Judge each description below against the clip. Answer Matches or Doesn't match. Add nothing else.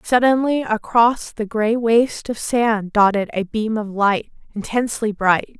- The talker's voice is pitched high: Matches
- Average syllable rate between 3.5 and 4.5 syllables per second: Matches